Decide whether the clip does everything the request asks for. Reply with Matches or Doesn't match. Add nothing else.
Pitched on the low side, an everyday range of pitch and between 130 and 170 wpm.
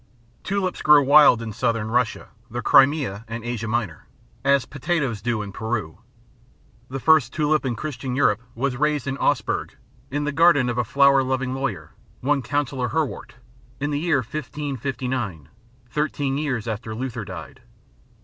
Matches